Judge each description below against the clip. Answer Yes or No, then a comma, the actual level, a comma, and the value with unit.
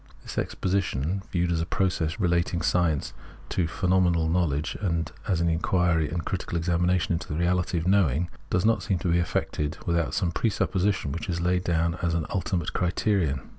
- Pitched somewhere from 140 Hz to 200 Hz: No, very low, 85 Hz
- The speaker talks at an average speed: Yes, average, 190 wpm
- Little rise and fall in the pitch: Yes, narrow, 1.8 semitones